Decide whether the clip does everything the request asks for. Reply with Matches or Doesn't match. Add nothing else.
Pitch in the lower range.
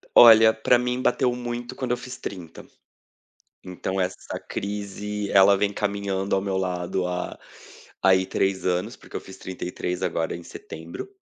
Matches